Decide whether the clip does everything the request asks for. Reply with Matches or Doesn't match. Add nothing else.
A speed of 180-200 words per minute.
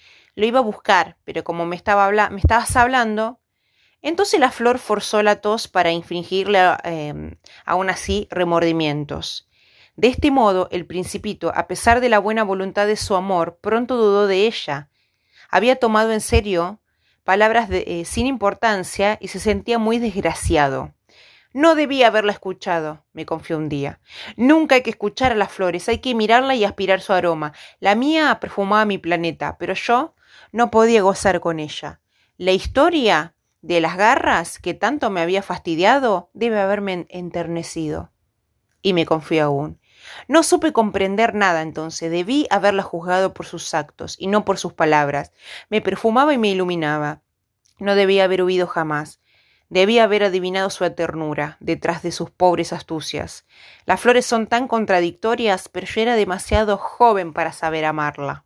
Doesn't match